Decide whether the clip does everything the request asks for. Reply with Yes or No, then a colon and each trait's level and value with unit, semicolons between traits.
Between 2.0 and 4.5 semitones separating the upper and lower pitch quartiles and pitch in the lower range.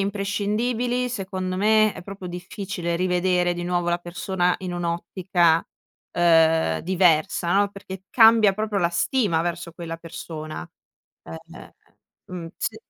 No: average, 2.7 semitones; medium, 180 Hz